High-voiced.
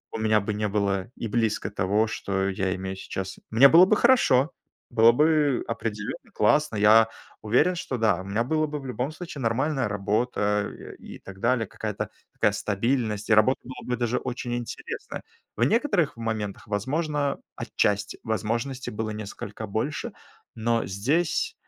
No: low, 115 Hz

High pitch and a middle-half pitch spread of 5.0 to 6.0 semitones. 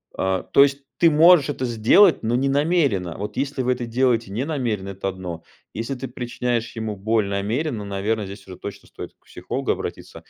No: low, 115 Hz; wide, 5.4 semitones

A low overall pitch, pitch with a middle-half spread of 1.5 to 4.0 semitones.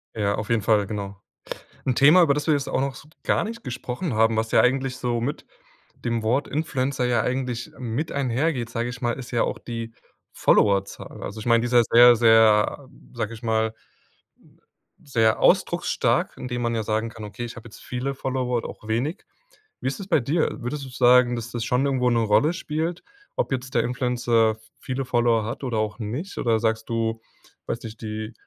Yes: low, 120 Hz; average, 2.8 semitones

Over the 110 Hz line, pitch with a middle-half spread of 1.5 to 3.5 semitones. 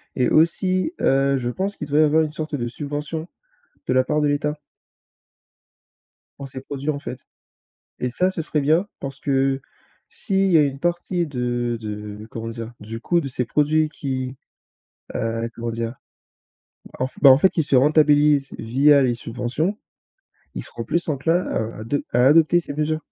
No: medium, 140 Hz; average, 4.0 semitones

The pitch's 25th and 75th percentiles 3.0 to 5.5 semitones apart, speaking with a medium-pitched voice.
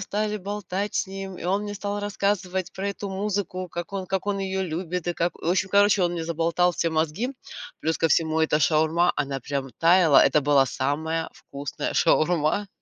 Yes: average, 3.7 semitones; medium, 180 Hz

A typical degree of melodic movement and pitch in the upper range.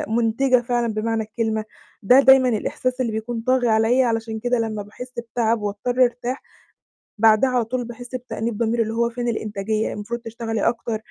No: narrow, 1.9 semitones; high, 230 Hz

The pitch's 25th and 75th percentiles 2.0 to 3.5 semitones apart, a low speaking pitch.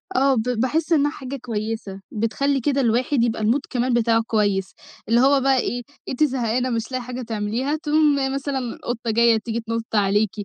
No: average, 3.2 semitones; high, 240 Hz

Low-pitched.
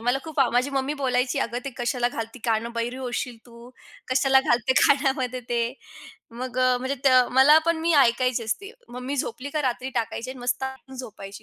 No: very high, 255 Hz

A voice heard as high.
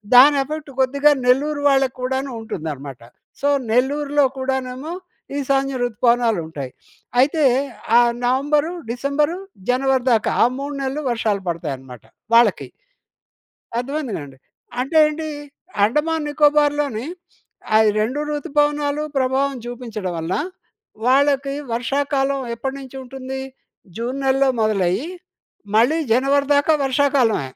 Yes: very high, 265 Hz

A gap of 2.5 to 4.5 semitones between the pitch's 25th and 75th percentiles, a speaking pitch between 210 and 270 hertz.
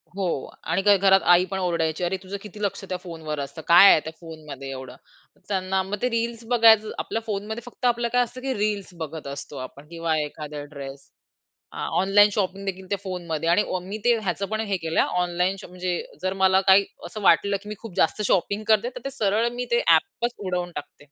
No: average, 4.1 semitones; high, 190 Hz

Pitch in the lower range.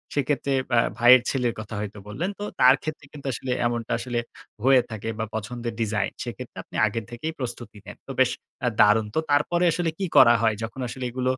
Yes: low, 120 Hz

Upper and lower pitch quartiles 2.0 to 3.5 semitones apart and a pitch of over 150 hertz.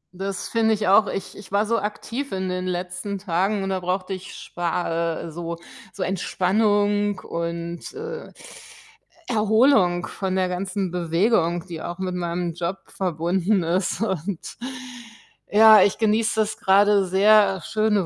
Yes: average, 2.9 semitones; high, 190 Hz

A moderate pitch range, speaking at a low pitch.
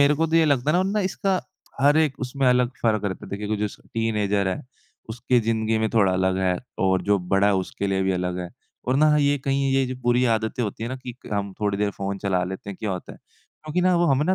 No: wide, 5.7 semitones; low, 110 Hz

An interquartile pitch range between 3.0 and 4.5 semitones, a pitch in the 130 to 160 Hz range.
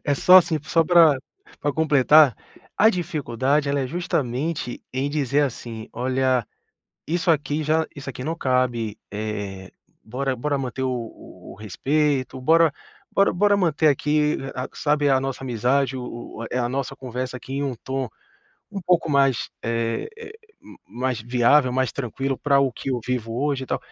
Yes: average, 3.3 semitones; low, 135 Hz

